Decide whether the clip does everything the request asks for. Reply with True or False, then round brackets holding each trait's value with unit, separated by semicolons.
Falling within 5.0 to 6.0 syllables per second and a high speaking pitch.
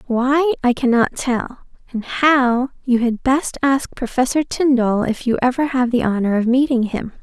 False (4.5 syllables/s; 250 Hz)